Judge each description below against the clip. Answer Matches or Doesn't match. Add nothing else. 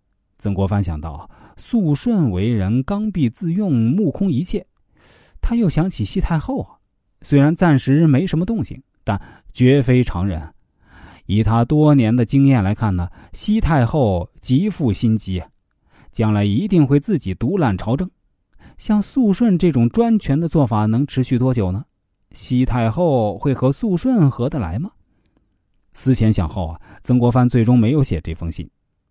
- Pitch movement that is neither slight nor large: Doesn't match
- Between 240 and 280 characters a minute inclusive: Doesn't match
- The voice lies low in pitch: Matches